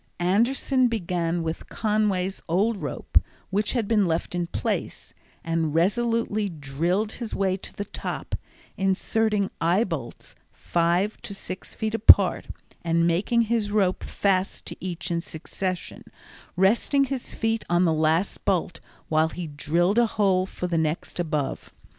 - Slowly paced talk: No, average, 145 wpm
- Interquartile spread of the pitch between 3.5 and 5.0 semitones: Yes, average, 4.2 semitones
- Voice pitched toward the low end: No, medium, 185 Hz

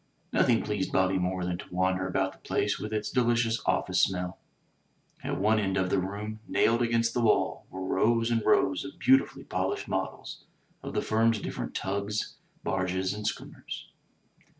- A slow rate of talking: No, average, 170 wpm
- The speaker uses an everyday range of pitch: Yes, average, 3.5 semitones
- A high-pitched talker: No, low, 105 Hz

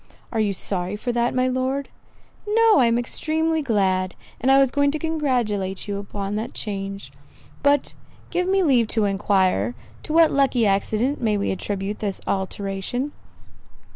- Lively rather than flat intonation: Yes, wide, 5.9 semitones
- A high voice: Yes, high, 230 Hz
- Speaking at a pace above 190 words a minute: No, average, 160 wpm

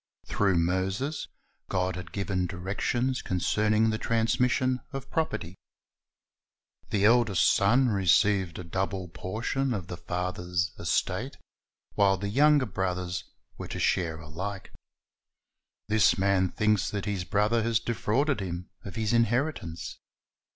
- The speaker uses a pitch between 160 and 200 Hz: No, low, 100 Hz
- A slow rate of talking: Yes, slow, 125 wpm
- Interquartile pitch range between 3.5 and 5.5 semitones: Yes, average, 4.0 semitones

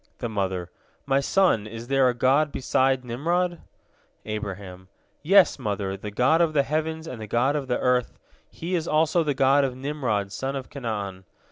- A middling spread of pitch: No, wide, 6.0 semitones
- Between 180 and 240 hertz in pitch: No, low, 130 Hz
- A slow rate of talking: No, average, 175 wpm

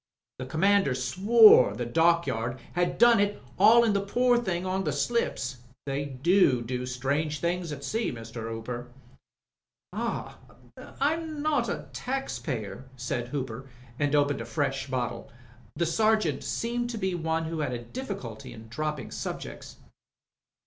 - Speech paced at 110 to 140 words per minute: No, average, 150 wpm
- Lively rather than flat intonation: Yes, wide, 8.2 semitones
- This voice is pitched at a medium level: Yes, medium, 155 Hz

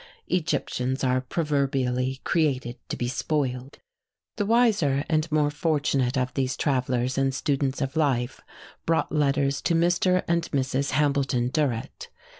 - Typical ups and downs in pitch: Yes, average, 3.1 semitones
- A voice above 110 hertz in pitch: Yes, medium, 140 Hz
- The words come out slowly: Yes, slow, 130 wpm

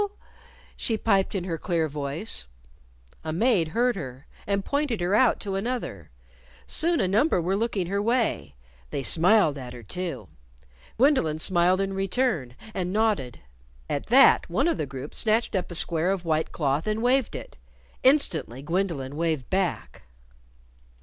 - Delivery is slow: No, average, 155 wpm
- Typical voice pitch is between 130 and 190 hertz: Yes, medium, 185 Hz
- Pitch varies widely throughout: Yes, wide, 6.1 semitones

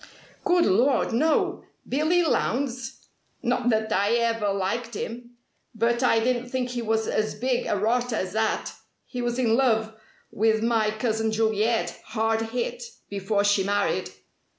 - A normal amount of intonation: No, narrow, 2.2 semitones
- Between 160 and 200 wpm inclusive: No, average, 150 wpm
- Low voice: No, high, 225 Hz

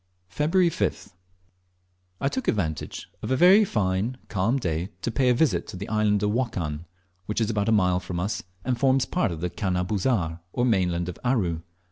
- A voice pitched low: Yes, low, 105 Hz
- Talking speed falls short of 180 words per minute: No, average, 190 wpm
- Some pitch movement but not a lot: No, wide, 6.0 semitones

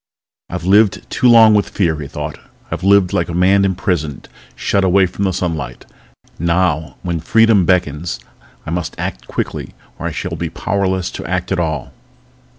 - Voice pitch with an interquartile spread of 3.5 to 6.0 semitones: No, average, 3.1 semitones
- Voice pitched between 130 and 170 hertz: No, very low, 90 Hz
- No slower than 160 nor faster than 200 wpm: Yes, average, 170 wpm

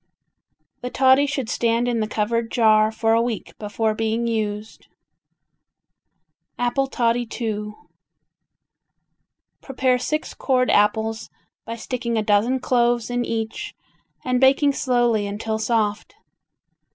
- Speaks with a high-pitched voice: Yes, high, 230 Hz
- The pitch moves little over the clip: Yes, narrow, 2.3 semitones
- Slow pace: Yes, slow, 115 wpm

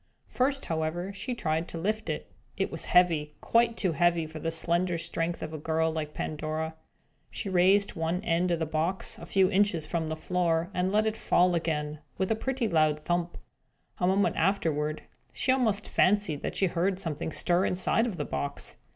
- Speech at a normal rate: Yes, average, 190 wpm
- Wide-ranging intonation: No, average, 3.4 semitones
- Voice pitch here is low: No, medium, 175 Hz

